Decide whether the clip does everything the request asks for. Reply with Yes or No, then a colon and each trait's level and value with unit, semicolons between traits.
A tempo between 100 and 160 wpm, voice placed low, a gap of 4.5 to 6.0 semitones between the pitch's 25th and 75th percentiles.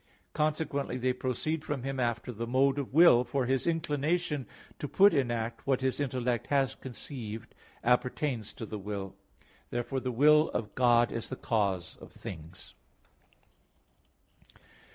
No: average, 145 wpm; low, 130 Hz; average, 3.4 semitones